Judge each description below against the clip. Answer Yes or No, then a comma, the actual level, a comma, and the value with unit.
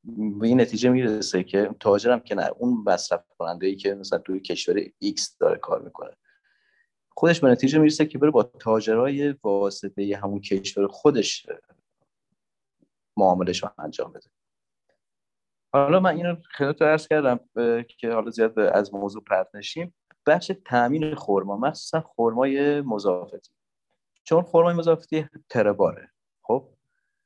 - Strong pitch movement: Yes, wide, 7.6 semitones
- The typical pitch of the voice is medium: Yes, medium, 145 Hz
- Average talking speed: Yes, average, 135 wpm